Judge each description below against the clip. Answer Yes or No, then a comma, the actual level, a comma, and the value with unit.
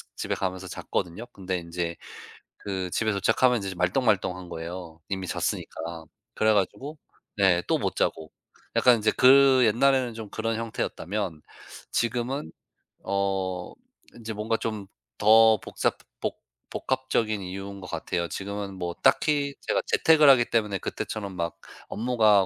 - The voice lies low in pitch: Yes, low, 100 Hz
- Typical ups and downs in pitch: Yes, average, 3.9 semitones